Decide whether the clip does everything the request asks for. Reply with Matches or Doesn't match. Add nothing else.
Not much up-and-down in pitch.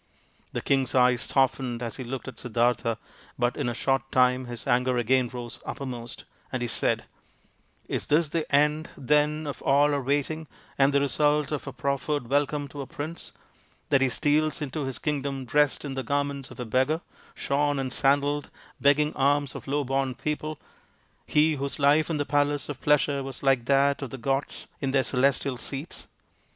Matches